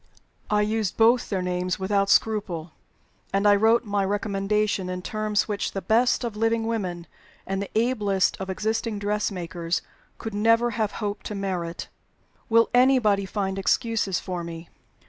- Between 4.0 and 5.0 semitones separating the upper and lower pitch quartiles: No, average, 2.7 semitones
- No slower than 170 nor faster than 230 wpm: No, average, 150 wpm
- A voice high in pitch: Yes, high, 205 Hz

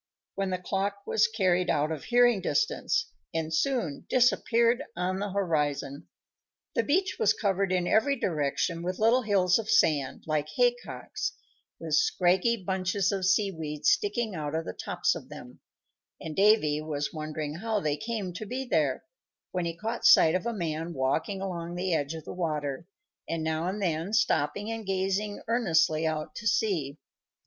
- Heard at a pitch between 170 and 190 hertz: Yes, medium, 185 Hz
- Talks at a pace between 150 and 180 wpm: Yes, average, 170 wpm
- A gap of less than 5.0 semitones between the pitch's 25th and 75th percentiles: No, average, 5.3 semitones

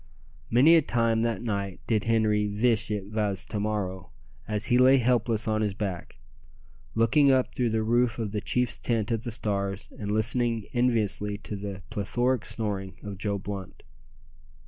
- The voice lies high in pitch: No, low, 110 Hz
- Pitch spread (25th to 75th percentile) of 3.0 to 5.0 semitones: No, narrow, 2.5 semitones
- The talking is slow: No, average, 170 wpm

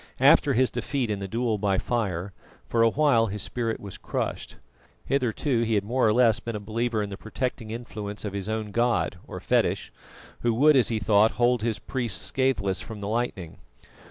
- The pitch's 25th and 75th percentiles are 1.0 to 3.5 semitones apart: Yes, average, 2.9 semitones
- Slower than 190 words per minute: No, average, 195 wpm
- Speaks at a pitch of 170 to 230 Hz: No, low, 115 Hz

